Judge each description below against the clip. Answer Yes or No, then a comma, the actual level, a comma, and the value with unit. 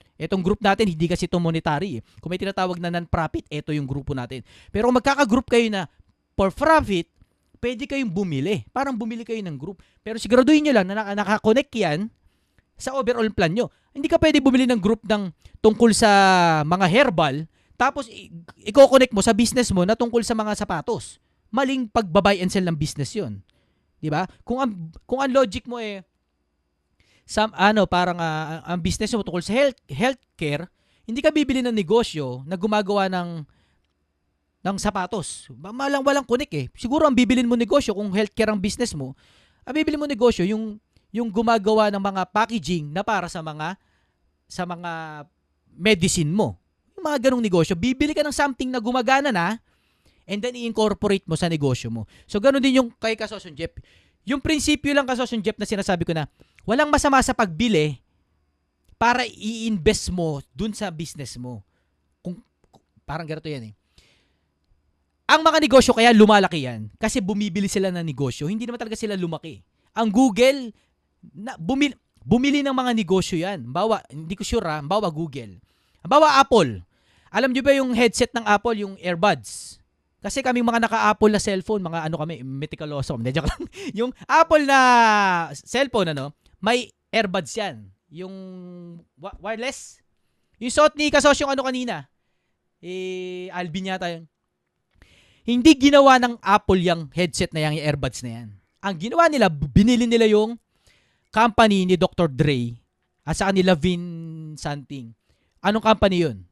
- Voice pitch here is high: Yes, high, 200 Hz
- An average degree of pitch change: No, wide, 7.3 semitones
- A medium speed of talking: No, fast, 165 wpm